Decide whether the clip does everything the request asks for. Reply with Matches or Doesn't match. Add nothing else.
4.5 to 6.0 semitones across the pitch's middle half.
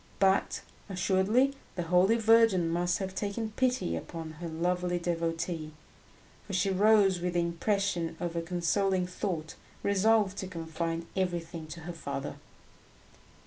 Doesn't match